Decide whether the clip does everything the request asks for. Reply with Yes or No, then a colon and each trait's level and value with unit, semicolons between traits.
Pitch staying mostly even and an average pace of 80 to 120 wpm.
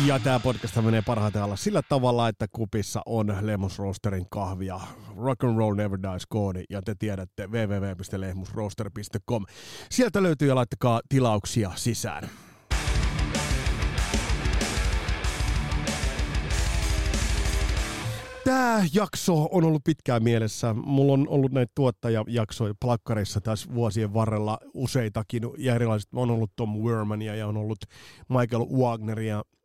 No: average, 3.7 semitones; average, 115 wpm